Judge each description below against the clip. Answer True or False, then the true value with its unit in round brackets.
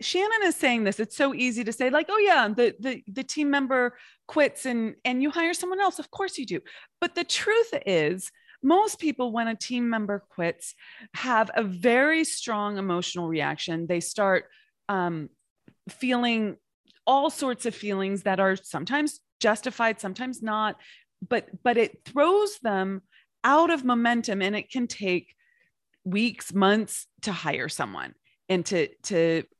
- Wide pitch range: True (6.6 semitones)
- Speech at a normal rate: True (160 wpm)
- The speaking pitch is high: True (240 Hz)